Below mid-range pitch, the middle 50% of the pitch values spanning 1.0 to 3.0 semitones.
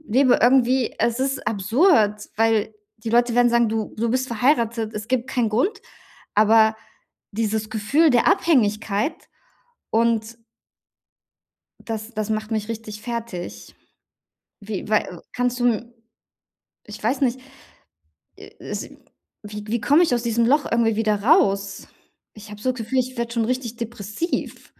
No: high, 230 Hz; narrow, 2.4 semitones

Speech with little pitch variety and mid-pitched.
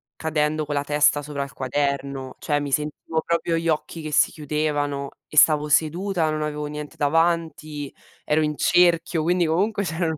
Yes: narrow, 1.9 semitones; medium, 150 Hz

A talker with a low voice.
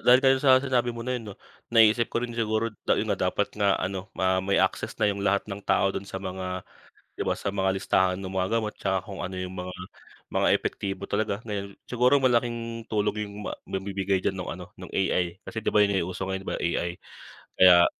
Yes: low, 100 Hz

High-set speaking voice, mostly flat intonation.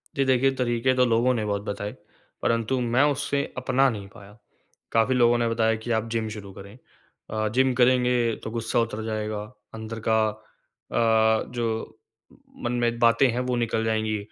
No: low, 115 Hz; narrow, 2.2 semitones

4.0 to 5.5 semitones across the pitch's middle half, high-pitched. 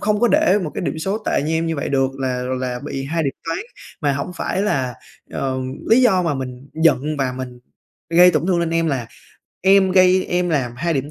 No: average, 5.1 semitones; medium, 160 Hz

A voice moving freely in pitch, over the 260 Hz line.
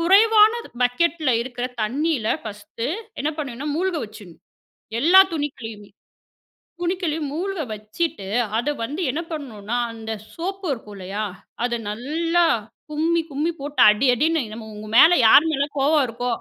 Yes: wide, 6.5 semitones; very high, 280 Hz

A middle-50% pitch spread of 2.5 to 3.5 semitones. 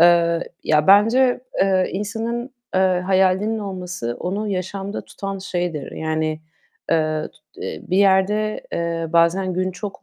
Yes: average, 2.9 semitones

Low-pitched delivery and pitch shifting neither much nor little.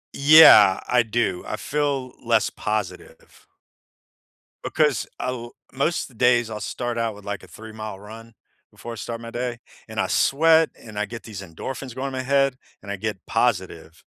Yes: low, 115 Hz; average, 3.5 semitones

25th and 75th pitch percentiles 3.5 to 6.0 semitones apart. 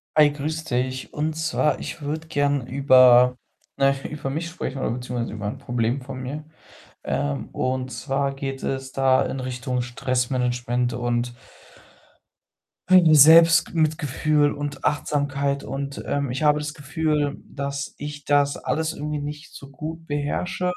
No: average, 2.8 semitones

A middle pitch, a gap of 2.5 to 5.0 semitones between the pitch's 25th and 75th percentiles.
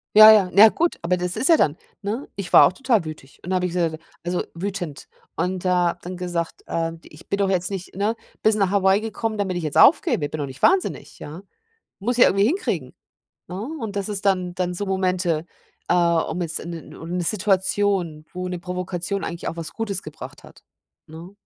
Yes: medium, 180 Hz; average, 2.9 semitones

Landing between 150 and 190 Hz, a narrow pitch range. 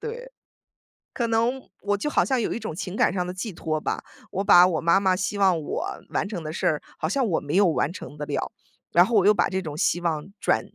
No: medium, 185 Hz; average, 4.1 semitones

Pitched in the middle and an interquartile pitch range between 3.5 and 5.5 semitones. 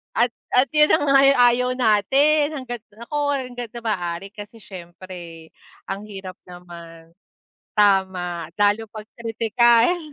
No: high, 215 Hz; average, 4.9 semitones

